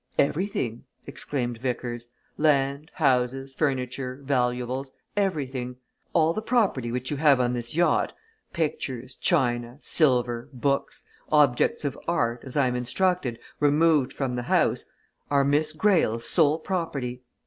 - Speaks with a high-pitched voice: No, low, 135 Hz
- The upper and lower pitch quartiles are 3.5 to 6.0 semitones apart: Yes, average, 3.8 semitones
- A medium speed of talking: No, slow, 125 wpm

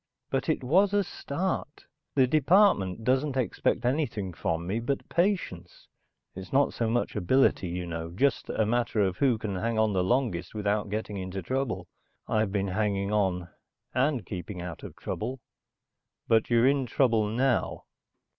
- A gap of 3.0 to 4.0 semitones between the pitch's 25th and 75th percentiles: No, wide, 5.6 semitones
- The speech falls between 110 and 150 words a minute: No, average, 160 wpm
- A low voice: Yes, low, 110 Hz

